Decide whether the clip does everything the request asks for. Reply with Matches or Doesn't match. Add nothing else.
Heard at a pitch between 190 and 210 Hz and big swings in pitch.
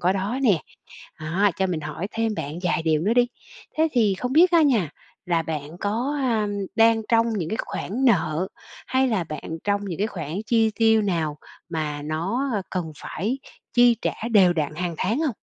Matches